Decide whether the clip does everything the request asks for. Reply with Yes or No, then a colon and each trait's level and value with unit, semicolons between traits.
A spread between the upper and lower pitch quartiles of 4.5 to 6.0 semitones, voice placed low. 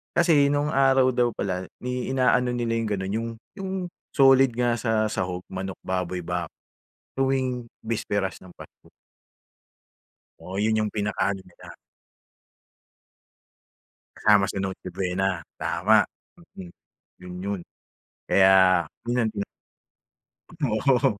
Yes: average, 5.0 semitones; low, 105 Hz